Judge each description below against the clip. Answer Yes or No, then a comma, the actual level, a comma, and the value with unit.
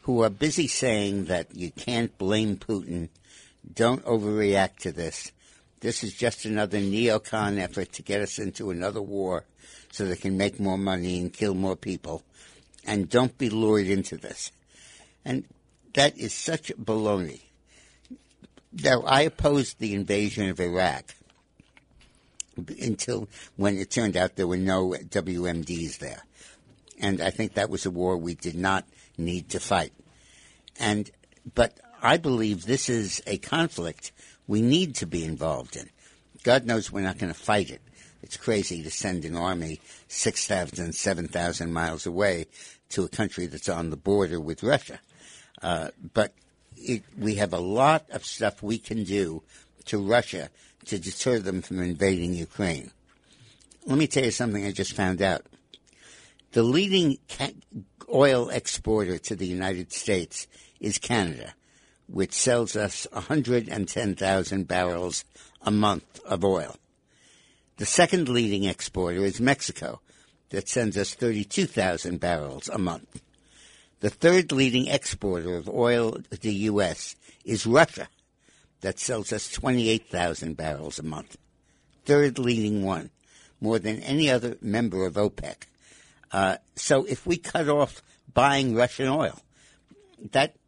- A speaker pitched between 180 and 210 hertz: No, low, 100 Hz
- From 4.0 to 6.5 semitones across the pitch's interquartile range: Yes, average, 4.4 semitones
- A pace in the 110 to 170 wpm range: Yes, average, 145 wpm